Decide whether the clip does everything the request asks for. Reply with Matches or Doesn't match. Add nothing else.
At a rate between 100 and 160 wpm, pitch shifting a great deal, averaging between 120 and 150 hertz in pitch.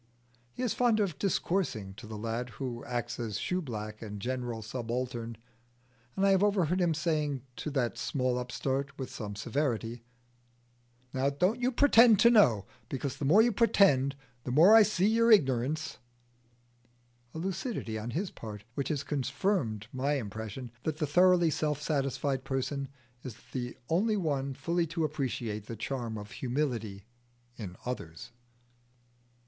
Matches